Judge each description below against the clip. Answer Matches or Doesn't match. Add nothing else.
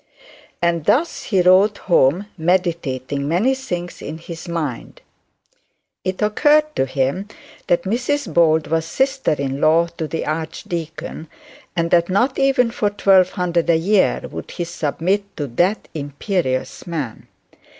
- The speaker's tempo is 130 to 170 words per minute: Matches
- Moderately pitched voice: Matches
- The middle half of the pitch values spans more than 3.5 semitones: Matches